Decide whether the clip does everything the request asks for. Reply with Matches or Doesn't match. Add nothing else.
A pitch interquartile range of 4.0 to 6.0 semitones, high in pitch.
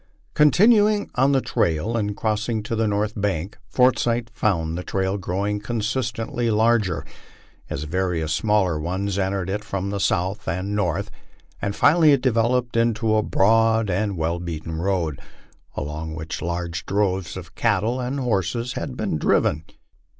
Doesn't match